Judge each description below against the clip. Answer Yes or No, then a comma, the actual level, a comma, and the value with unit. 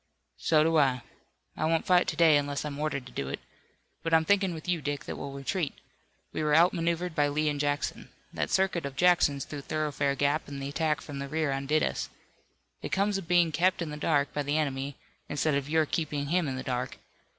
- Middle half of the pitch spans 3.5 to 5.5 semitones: No, average, 2.7 semitones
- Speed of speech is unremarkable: No, fast, 220 wpm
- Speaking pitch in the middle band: Yes, medium, 150 Hz